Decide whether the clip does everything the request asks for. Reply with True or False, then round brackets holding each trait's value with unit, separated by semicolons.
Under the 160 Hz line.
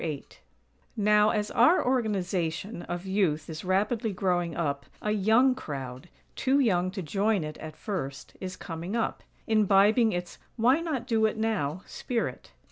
False (195 Hz)